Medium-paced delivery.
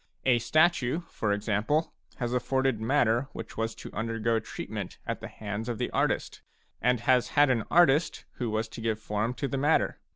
Yes: average, 185 wpm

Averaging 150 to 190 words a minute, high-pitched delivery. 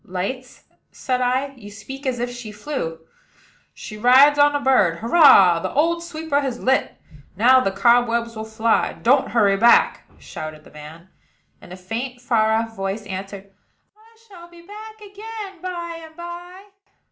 Yes: average, 160 wpm; very high, 250 Hz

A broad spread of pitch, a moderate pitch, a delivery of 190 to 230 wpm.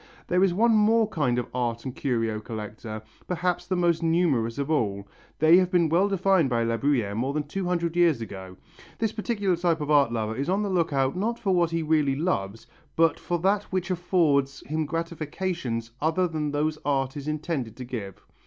Yes: wide, 6.3 semitones; medium, 155 Hz; average, 200 wpm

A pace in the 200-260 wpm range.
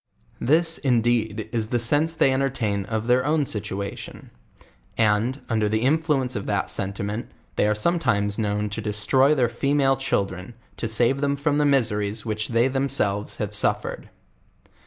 No: average, 155 wpm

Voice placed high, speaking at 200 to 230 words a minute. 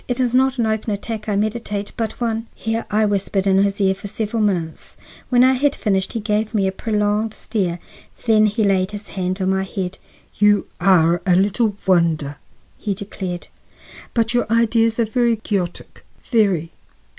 No: high, 210 Hz; average, 180 wpm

